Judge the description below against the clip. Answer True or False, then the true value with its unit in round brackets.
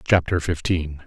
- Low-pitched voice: True (85 Hz)